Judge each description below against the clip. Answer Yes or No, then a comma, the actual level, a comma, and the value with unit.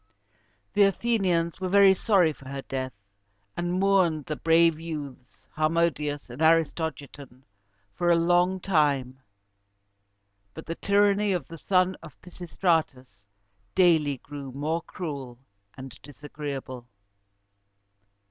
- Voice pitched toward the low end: No, medium, 160 Hz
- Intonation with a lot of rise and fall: No, average, 4.2 semitones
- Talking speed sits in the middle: No, slow, 110 wpm